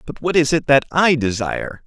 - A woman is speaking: No, male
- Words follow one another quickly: Yes, fast, 225 wpm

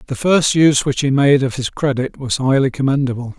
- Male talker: Yes, male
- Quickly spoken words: Yes, fast, 215 wpm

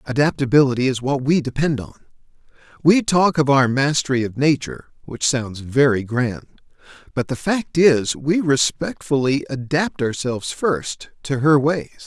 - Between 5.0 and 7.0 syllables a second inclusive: No, 4.6 syllables/s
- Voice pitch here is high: No, medium, 140 Hz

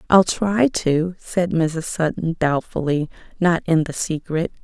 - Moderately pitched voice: Yes, medium, 170 Hz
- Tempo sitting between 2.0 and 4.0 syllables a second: Yes, 3.8 syllables/s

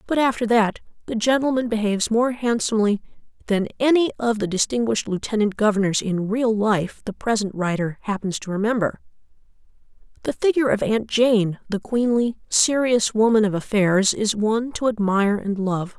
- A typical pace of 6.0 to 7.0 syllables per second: No, 5.3 syllables/s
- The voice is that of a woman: Yes, female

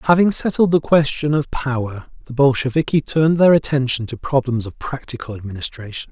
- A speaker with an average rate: Yes, average, 155 wpm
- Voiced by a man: Yes, male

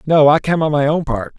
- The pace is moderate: No, fast, 305 wpm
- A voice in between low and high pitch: Yes, medium, 150 Hz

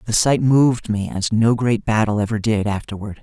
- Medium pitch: No, low, 110 Hz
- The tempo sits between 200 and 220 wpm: Yes, fast, 205 wpm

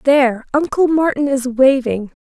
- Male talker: No, female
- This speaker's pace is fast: No, slow, 135 wpm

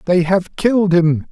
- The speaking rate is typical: Yes, average, 185 wpm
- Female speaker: No, male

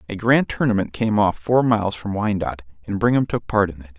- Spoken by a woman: No, male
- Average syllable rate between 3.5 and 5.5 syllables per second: No, 5.9 syllables/s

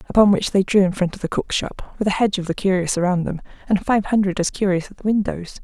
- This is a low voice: No, high, 190 Hz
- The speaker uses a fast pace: Yes, fast, 275 wpm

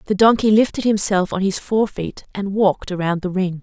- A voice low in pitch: No, high, 195 Hz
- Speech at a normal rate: No, fast, 215 wpm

